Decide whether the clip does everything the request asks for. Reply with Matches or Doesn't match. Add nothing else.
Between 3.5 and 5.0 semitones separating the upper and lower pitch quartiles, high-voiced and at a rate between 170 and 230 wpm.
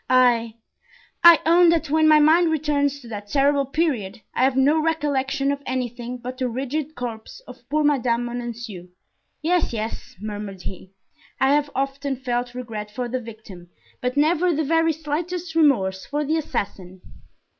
Doesn't match